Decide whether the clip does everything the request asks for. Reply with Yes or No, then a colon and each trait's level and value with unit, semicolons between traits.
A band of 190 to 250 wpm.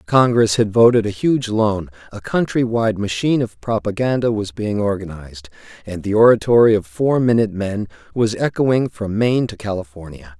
No: average, 160 wpm